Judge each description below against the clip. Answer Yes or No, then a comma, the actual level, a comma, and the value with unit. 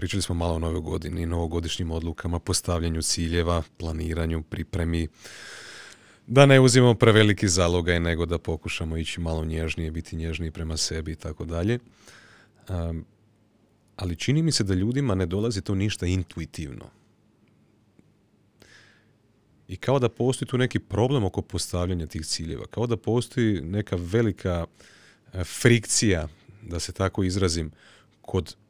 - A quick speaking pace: No, average, 135 wpm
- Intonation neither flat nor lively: Yes, average, 4.7 semitones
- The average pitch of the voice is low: Yes, very low, 90 Hz